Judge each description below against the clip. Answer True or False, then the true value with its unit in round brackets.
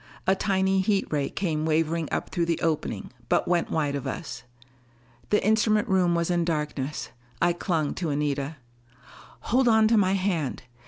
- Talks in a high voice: False (170 Hz)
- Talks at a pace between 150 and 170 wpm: True (165 wpm)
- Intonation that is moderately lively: True (4.0 semitones)